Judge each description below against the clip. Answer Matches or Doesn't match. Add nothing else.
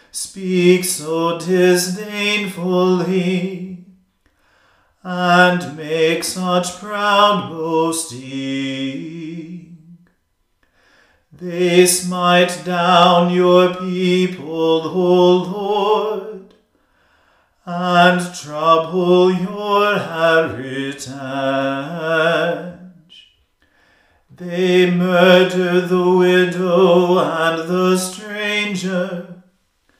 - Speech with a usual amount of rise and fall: Doesn't match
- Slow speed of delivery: Matches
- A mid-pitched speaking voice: Matches